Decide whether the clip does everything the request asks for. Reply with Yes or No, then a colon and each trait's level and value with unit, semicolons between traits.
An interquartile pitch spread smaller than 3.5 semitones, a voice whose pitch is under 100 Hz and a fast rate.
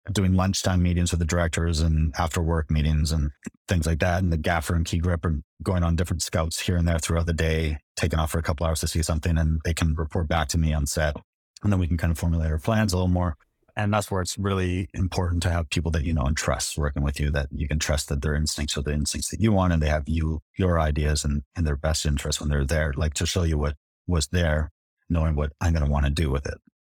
Yes: narrow, 2.5 semitones; very low, 80 Hz; fast, 275 wpm